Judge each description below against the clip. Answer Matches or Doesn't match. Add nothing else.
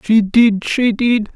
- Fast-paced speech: Doesn't match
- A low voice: Doesn't match